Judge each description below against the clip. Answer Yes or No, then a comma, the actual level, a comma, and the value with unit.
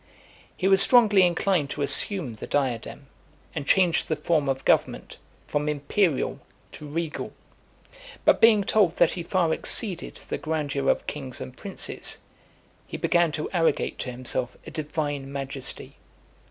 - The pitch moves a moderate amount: Yes, average, 4.4 semitones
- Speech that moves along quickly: No, average, 145 wpm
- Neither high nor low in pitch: Yes, medium, 155 Hz